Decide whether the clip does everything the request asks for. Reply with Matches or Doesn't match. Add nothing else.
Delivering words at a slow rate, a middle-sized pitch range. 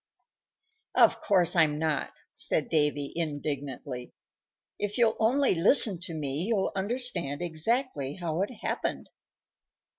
Doesn't match